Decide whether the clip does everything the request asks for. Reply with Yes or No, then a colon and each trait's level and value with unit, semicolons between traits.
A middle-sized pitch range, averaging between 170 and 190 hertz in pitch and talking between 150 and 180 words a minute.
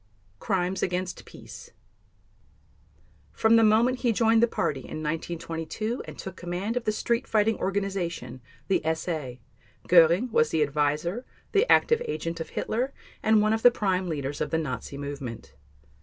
No: wide, 5.9 semitones; medium, 185 Hz; average, 155 wpm